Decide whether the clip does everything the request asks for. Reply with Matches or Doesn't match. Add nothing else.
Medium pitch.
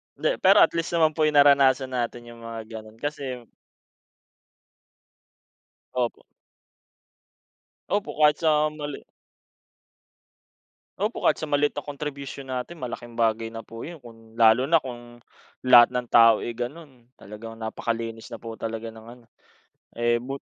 Doesn't match